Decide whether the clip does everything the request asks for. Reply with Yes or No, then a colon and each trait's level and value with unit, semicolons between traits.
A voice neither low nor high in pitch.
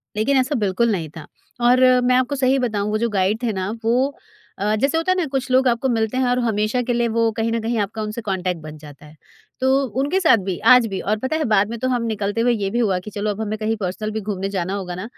No: high, 220 Hz